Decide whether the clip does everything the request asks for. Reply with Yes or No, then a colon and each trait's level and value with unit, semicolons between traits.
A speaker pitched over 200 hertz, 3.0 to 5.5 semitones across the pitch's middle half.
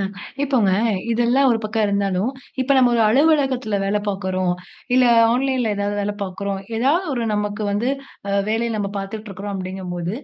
Yes: high, 210 Hz; average, 3.9 semitones